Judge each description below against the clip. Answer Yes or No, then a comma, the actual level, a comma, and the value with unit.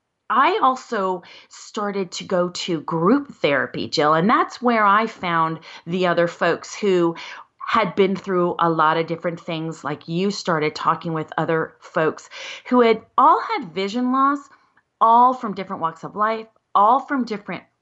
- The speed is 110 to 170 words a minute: Yes, average, 160 wpm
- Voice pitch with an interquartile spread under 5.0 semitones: No, average, 5.3 semitones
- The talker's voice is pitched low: No, high, 190 Hz